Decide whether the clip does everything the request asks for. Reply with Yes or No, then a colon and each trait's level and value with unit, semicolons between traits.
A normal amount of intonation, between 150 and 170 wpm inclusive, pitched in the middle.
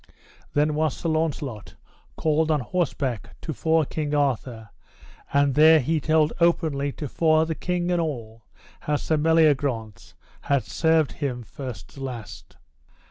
No: average, 3.2 semitones; average, 140 wpm; medium, 150 Hz